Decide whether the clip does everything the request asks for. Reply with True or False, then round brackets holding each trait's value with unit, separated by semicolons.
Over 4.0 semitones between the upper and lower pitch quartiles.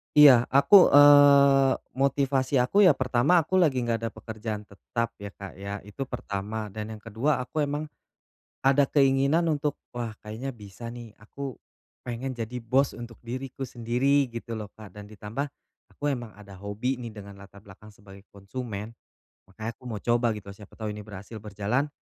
True (4.4 semitones)